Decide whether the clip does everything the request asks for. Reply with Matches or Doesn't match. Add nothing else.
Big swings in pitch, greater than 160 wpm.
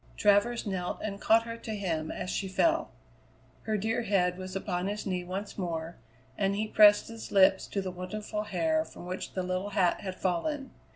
Doesn't match